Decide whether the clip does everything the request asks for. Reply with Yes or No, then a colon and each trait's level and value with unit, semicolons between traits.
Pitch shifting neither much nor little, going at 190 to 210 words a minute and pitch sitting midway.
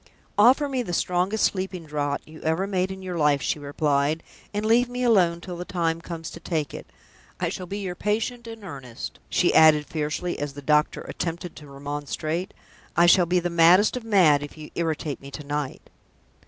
Yes: average, 4.2 semitones; average, 200 wpm; medium, 170 Hz